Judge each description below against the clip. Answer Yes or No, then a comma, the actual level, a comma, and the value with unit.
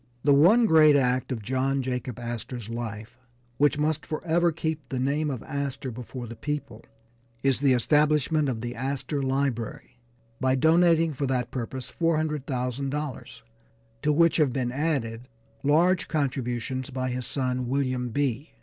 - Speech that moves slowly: No, average, 145 wpm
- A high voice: No, low, 135 Hz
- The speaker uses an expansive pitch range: No, average, 3.2 semitones